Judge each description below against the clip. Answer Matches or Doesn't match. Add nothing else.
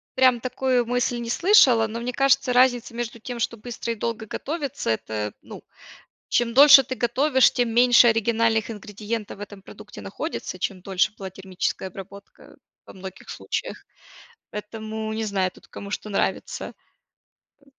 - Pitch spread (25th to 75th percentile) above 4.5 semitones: Doesn't match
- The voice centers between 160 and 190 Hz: Doesn't match